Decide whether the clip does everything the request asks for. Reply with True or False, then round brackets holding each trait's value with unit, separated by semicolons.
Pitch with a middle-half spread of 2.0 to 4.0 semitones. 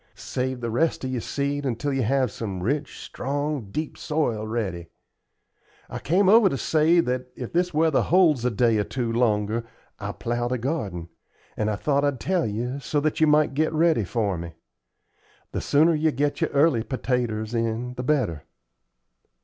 False (5.0 semitones)